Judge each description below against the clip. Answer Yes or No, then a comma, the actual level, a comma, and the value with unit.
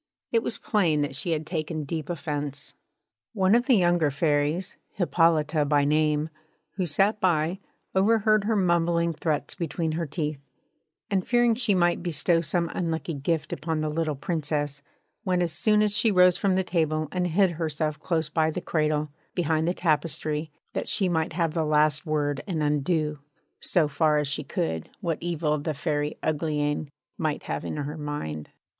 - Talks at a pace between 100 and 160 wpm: No, average, 170 wpm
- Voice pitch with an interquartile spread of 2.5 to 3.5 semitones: Yes, average, 2.8 semitones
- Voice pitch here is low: No, medium, 160 Hz